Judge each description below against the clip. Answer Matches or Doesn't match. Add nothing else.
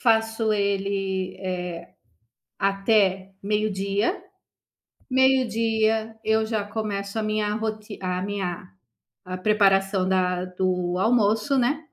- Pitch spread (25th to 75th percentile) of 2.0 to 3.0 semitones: Matches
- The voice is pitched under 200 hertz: Doesn't match